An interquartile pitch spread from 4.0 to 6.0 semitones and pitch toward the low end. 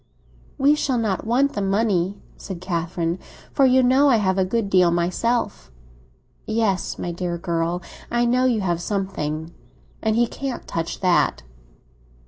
No: wide, 5.5 semitones; high, 195 Hz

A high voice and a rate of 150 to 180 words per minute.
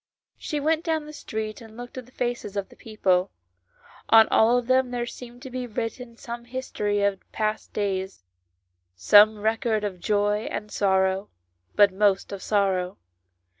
Yes: high, 215 Hz; average, 165 wpm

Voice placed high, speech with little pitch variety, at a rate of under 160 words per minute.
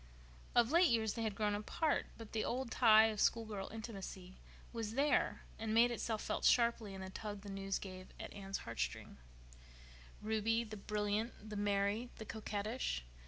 No: high, 215 Hz; narrow, 2.2 semitones; average, 170 wpm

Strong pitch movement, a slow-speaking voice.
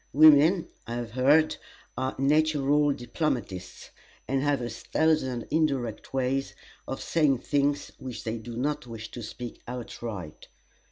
No: average, 3.7 semitones; slow, 130 wpm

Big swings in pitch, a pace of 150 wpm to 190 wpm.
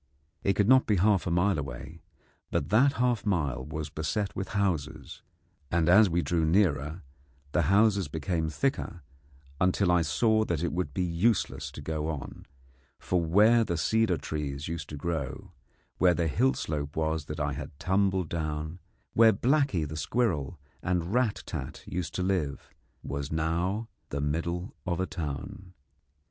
No: average, 4.5 semitones; average, 160 wpm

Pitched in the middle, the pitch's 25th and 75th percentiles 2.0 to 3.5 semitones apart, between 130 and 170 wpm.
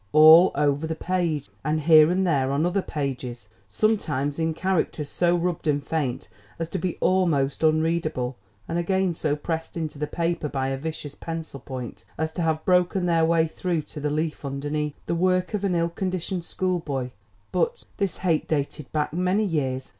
No: medium, 160 Hz; average, 3.2 semitones; average, 180 wpm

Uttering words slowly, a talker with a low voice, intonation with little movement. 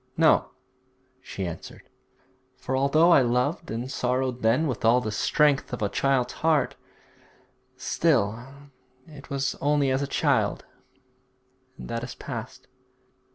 No: slow, 130 wpm; low, 130 Hz; average, 3.1 semitones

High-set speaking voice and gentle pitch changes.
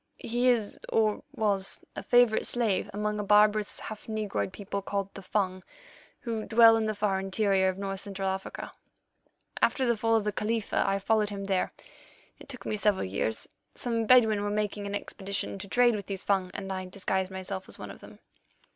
Yes: high, 205 Hz; narrow, 2.1 semitones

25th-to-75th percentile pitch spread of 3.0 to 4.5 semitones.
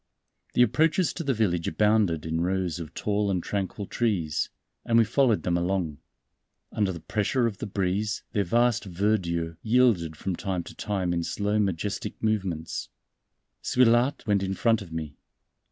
Yes: average, 4.2 semitones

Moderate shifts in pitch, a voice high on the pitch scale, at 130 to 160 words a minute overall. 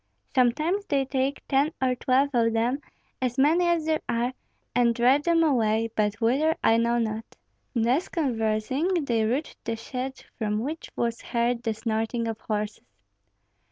Yes: average, 3.7 semitones; high, 245 Hz; average, 155 wpm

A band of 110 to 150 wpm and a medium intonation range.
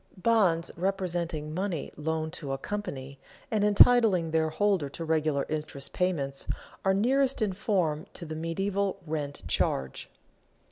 Yes: slow, 135 wpm; average, 4.5 semitones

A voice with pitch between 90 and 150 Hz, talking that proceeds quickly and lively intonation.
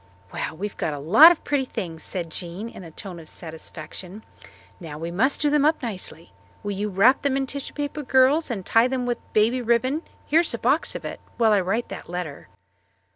No: high, 220 Hz; fast, 210 wpm; wide, 7.0 semitones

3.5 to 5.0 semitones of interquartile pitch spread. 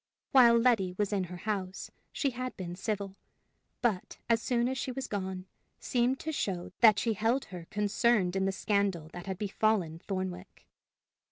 Yes: average, 4.1 semitones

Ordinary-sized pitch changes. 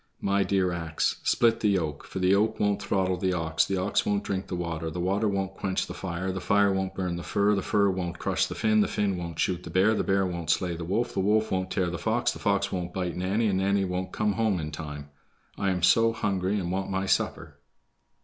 No: narrow, 2.2 semitones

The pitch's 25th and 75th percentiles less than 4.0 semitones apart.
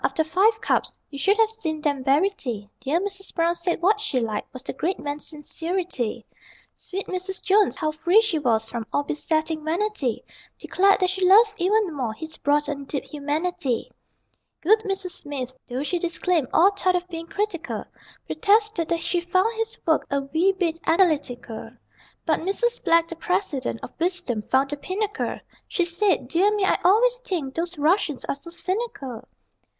No: average, 5.2 semitones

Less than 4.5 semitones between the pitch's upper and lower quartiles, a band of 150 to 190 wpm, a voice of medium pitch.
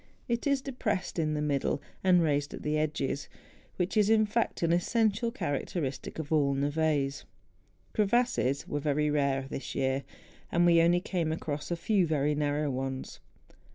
No: average, 4.8 semitones; average, 165 wpm; medium, 155 Hz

